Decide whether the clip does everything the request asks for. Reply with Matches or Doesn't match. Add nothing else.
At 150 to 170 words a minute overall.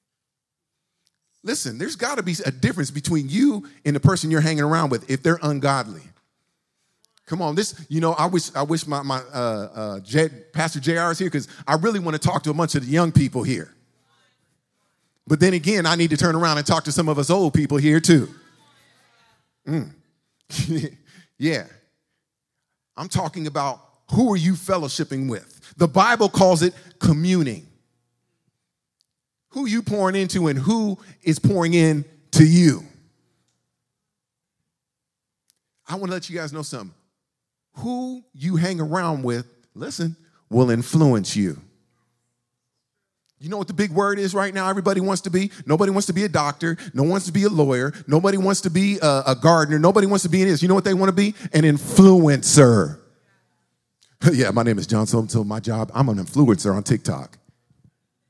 Doesn't match